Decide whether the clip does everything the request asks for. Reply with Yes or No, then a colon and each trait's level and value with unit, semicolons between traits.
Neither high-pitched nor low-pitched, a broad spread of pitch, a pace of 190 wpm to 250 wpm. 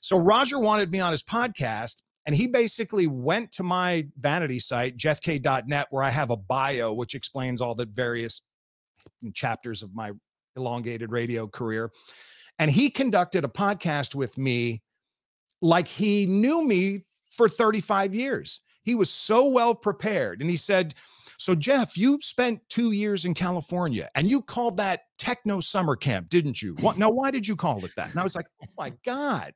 No: medium, 175 Hz; wide, 8.6 semitones; average, 175 wpm